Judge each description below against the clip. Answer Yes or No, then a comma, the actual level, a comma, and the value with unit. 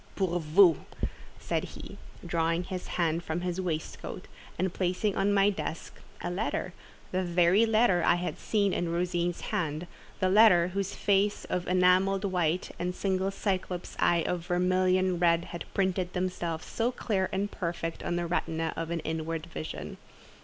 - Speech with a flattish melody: Yes, narrow, 1.9 semitones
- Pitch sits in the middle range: Yes, medium, 180 Hz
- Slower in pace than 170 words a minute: Yes, average, 155 wpm